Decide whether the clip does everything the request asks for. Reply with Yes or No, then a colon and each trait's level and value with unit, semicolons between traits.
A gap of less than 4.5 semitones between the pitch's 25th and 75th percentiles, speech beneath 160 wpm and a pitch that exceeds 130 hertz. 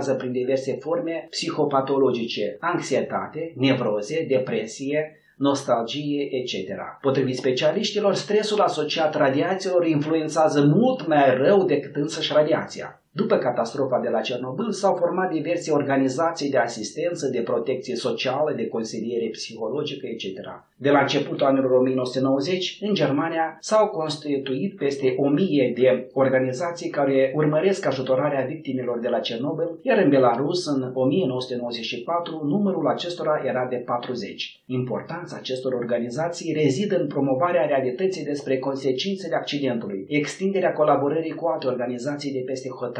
Yes: average, 3.9 semitones; average, 120 wpm; medium, 140 Hz